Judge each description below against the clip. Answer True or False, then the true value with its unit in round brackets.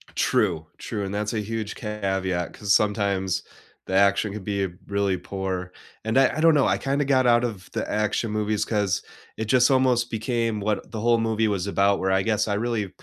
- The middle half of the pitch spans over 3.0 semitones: False (2.6 semitones)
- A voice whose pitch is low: True (105 Hz)